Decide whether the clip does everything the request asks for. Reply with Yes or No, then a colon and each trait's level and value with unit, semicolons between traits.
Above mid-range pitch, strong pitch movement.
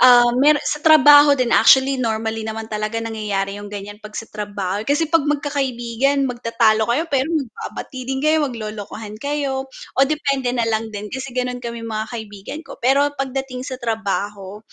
No: high, 240 Hz; average, 4.1 semitones